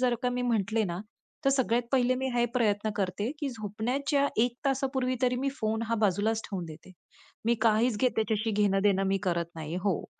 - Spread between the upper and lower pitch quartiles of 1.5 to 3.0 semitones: No, average, 3.7 semitones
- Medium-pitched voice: No, high, 225 Hz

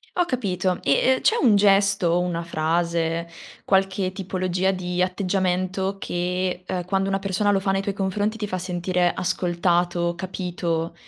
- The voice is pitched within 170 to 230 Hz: Yes, medium, 185 Hz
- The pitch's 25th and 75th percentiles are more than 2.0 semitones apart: No, narrow, 1.7 semitones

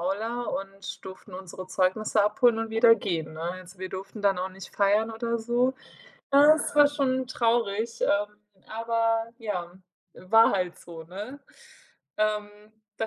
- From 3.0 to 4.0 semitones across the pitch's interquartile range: Yes, average, 3.5 semitones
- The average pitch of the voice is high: Yes, high, 215 Hz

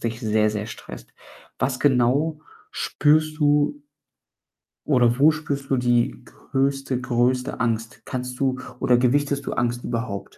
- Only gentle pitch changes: No, average, 3.0 semitones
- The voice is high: No, low, 125 Hz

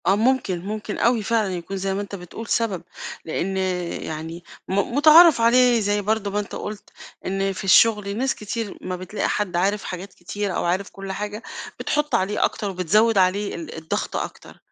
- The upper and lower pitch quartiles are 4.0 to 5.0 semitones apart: No, average, 2.9 semitones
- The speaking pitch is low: No, high, 200 Hz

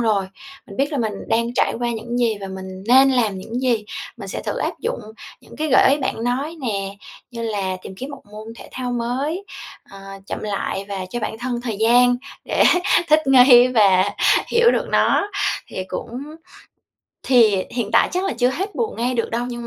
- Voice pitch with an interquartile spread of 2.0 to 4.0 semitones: Yes, average, 3.6 semitones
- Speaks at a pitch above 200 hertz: Yes, high, 240 Hz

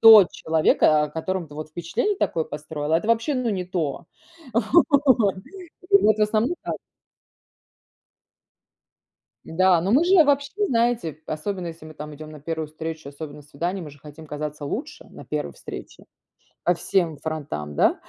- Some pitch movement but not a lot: No, wide, 6.1 semitones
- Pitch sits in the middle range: Yes, medium, 165 Hz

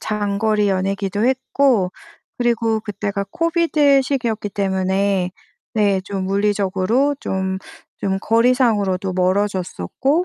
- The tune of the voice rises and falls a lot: No, average, 3.8 semitones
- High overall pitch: Yes, high, 205 Hz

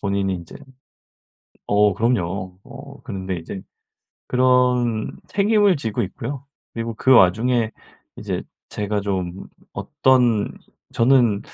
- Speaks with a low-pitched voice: Yes, low, 110 Hz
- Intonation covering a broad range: No, average, 4.5 semitones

